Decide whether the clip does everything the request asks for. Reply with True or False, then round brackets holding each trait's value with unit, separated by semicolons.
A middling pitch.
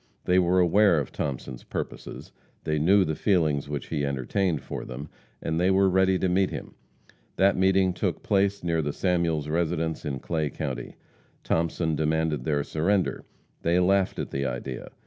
False (80 Hz)